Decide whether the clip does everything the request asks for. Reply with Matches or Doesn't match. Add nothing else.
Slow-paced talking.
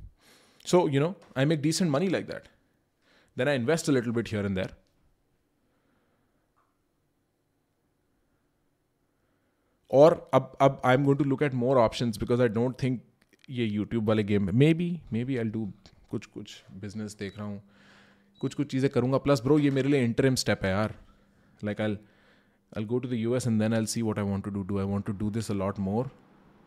Doesn't match